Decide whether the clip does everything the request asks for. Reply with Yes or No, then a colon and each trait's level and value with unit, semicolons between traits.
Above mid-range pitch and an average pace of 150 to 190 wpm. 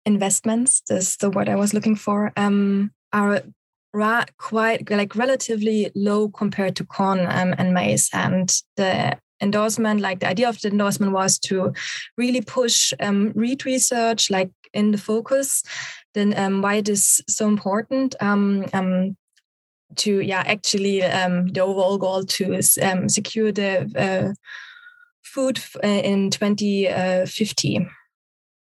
No: high, 205 Hz; slow, 135 wpm